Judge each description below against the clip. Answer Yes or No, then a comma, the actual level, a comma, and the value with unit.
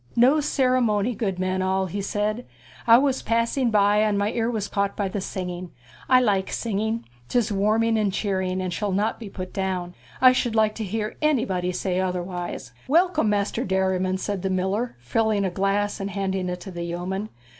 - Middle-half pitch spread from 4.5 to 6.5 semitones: No, average, 3.2 semitones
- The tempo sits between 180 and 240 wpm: Yes, average, 190 wpm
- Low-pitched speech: No, high, 200 Hz